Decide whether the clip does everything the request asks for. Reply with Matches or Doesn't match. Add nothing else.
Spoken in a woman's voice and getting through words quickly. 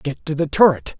Doesn't match